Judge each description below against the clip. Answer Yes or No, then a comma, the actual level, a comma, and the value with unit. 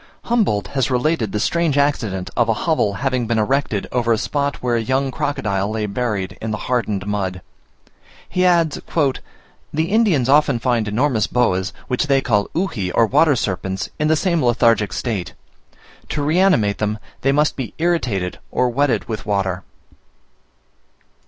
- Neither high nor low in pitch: No, low, 125 Hz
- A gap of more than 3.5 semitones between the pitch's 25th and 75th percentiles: Yes, wide, 5.6 semitones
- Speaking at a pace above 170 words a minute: No, average, 160 wpm